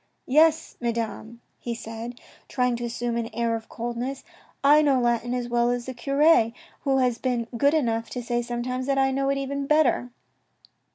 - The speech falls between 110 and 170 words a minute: No, average, 190 wpm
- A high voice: Yes, high, 245 Hz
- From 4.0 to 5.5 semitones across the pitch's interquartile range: No, narrow, 2.5 semitones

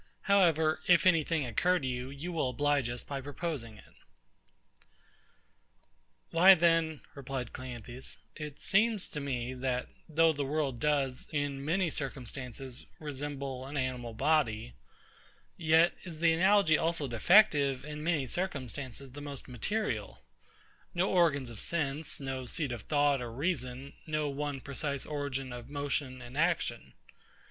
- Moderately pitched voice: Yes, medium, 145 Hz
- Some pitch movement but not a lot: Yes, average, 3.8 semitones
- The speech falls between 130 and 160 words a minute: Yes, average, 140 wpm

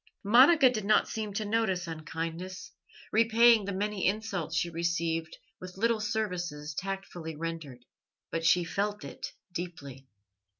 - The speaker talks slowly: Yes, slow, 130 wpm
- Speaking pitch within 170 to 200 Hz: Yes, medium, 185 Hz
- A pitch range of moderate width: Yes, average, 4.5 semitones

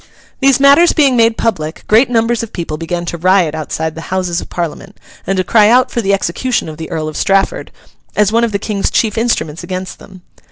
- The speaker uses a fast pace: Yes, fast, 215 wpm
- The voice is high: Yes, high, 195 Hz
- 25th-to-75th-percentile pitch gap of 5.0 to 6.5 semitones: Yes, average, 5.3 semitones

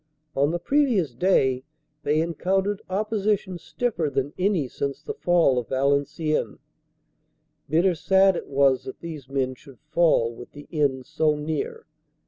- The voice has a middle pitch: Yes, medium, 155 Hz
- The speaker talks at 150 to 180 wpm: No, average, 140 wpm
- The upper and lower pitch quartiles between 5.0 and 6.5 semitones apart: Yes, average, 5.3 semitones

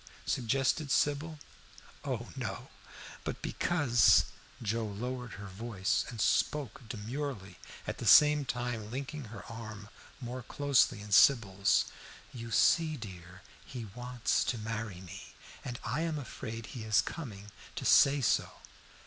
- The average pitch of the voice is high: No, low, 115 Hz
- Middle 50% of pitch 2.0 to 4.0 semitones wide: No, average, 4.4 semitones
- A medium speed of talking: No, slow, 130 wpm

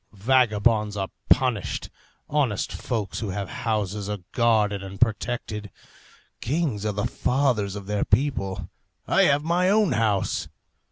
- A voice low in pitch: Yes, low, 110 Hz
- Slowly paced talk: Yes, slow, 130 wpm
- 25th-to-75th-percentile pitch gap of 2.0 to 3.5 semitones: No, average, 3.9 semitones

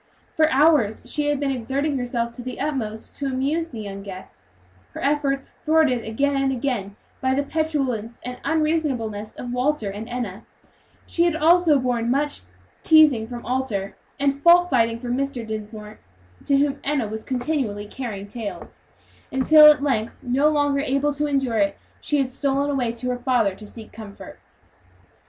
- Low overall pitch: No, very high, 260 Hz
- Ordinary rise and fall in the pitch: Yes, average, 4.3 semitones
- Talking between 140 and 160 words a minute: No, average, 170 wpm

